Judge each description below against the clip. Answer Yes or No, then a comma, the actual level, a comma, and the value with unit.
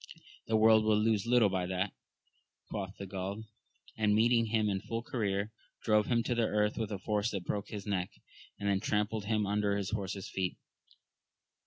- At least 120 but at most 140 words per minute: No, average, 190 wpm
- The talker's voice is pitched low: Yes, low, 105 Hz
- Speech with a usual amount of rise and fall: No, narrow, 1.9 semitones